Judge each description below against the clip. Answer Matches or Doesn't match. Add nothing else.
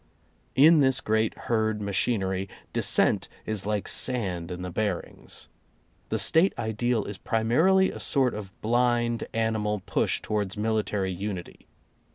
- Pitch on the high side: Doesn't match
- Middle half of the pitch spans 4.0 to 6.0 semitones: Doesn't match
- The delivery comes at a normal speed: Doesn't match